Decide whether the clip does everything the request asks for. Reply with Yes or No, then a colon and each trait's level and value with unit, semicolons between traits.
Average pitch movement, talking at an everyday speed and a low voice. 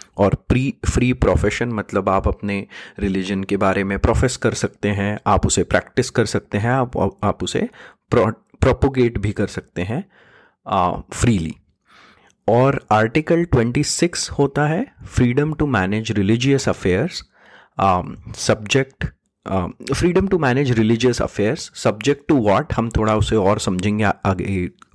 No: average, 4.6 semitones; slow, 130 wpm; low, 110 Hz